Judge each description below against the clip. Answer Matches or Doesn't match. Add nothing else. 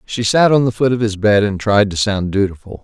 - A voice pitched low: Matches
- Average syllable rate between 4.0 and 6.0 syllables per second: Matches